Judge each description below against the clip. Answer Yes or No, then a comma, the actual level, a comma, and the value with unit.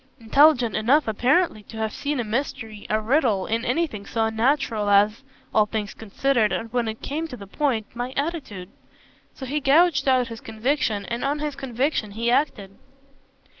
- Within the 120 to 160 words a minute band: No, average, 170 wpm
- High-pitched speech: Yes, high, 235 Hz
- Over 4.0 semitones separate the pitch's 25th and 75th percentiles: Yes, average, 4.4 semitones